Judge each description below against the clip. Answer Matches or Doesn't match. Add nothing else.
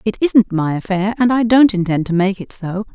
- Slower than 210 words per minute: Doesn't match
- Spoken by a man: Doesn't match